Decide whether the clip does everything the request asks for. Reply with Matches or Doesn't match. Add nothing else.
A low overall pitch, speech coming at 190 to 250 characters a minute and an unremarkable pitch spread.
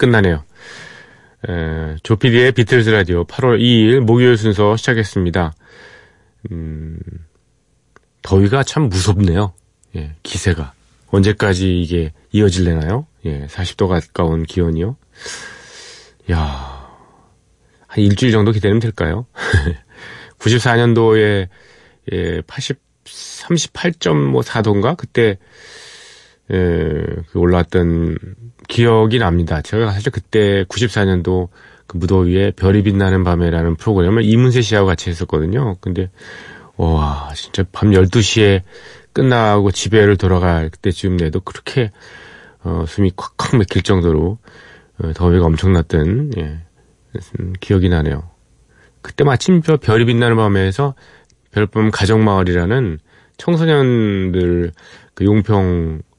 Matches